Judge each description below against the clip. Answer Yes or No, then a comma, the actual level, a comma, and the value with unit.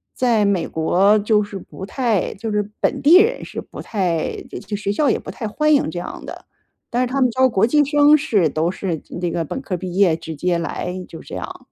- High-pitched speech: Yes, high, 205 Hz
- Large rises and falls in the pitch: Yes, wide, 6.3 semitones